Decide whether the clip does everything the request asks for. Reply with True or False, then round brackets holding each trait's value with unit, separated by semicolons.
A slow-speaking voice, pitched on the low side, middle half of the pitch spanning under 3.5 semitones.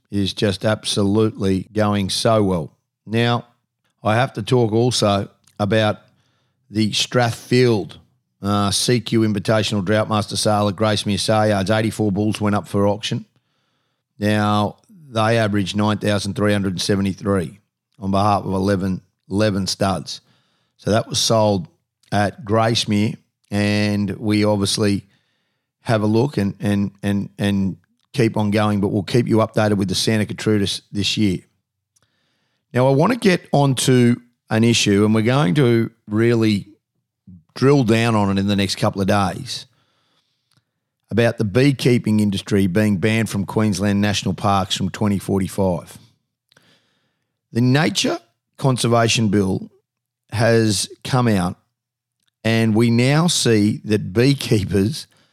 True (130 wpm; 110 Hz; 2.8 semitones)